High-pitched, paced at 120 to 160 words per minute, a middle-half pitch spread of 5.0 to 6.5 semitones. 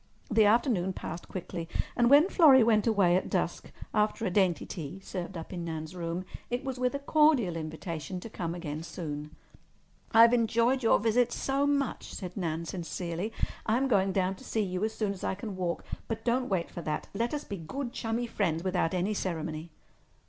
No: high, 195 Hz; average, 190 wpm; average, 5.3 semitones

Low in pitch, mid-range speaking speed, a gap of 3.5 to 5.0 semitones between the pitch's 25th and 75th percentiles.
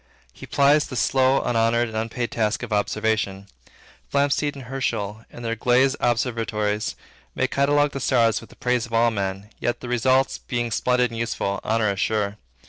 No: low, 115 Hz; average, 175 wpm; average, 3.0 semitones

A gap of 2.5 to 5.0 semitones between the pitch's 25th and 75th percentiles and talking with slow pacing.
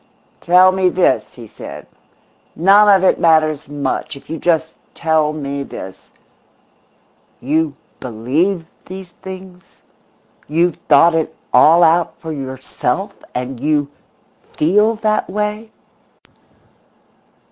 Yes: average, 4.5 semitones; slow, 110 wpm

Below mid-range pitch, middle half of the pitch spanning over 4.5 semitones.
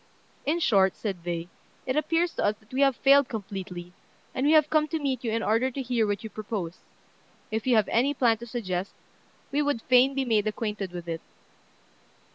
No: high, 230 Hz; average, 5.2 semitones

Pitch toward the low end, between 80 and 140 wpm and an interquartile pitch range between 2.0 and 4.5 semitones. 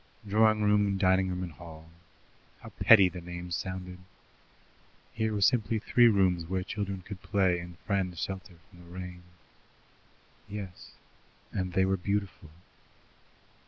Yes: very low, 95 Hz; slow, 135 wpm; narrow, 2.4 semitones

